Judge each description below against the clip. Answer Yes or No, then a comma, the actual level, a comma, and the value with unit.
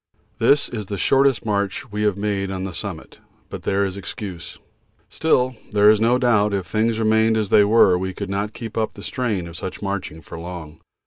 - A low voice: Yes, low, 105 Hz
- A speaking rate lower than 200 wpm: No, fast, 205 wpm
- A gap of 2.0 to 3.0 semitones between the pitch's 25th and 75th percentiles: Yes, narrow, 2.6 semitones